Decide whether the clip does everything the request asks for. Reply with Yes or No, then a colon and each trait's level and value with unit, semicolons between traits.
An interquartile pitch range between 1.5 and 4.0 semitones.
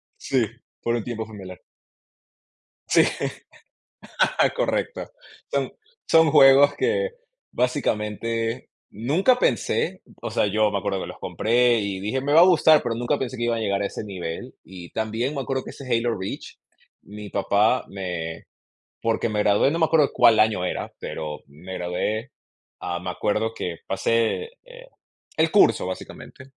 No: average, 5.1 semitones